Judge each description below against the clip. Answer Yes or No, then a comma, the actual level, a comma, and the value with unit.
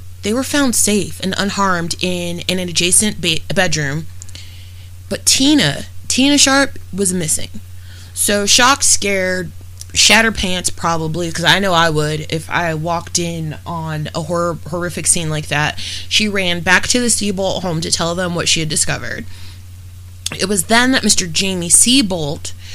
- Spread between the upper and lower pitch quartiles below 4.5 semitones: No, average, 4.9 semitones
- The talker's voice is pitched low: No, medium, 170 Hz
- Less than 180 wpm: Yes, average, 160 wpm